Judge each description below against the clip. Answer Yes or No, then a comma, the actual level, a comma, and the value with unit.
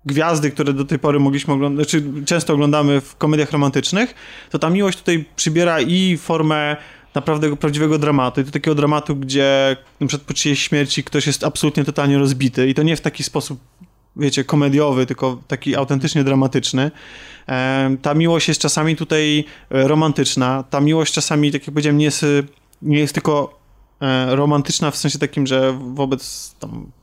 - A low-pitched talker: No, medium, 145 Hz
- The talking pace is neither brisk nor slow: No, fast, 165 wpm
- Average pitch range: No, narrow, 1.8 semitones